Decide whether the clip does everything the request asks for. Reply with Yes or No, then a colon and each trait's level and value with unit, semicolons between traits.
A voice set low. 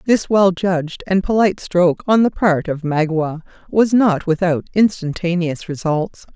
No: medium, 180 Hz